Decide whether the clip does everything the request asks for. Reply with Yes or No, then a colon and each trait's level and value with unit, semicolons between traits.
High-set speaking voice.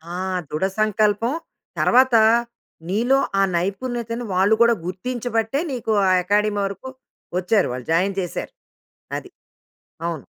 Yes: high, 215 Hz